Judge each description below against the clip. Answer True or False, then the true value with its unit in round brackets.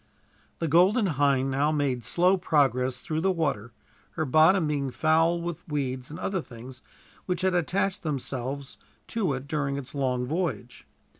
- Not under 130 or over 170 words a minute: True (155 wpm)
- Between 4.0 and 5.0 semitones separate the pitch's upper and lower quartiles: True (4.6 semitones)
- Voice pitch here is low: False (150 Hz)